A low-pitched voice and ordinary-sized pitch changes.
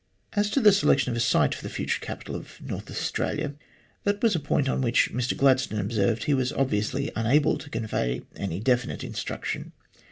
Yes: low, 130 Hz; average, 4.5 semitones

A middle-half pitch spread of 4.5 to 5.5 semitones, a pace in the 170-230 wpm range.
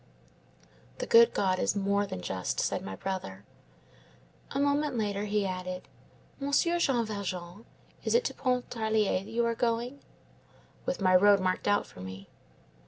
No: average, 5.0 semitones; average, 155 wpm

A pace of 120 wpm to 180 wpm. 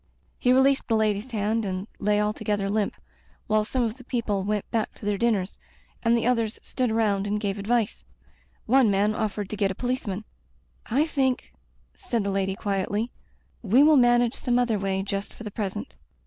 No: average, 195 wpm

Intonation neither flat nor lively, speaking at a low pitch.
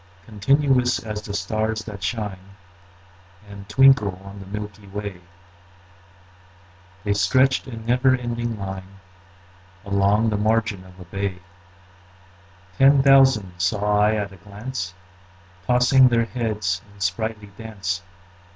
Yes: average, 3.1 semitones; low, 105 Hz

